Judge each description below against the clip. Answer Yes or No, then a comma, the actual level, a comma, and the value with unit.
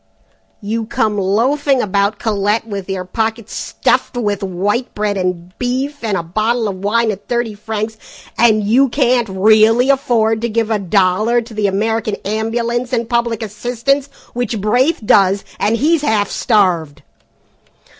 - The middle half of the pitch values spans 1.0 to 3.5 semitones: Yes, average, 2.9 semitones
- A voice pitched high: Yes, high, 220 Hz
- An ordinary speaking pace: Yes, average, 150 wpm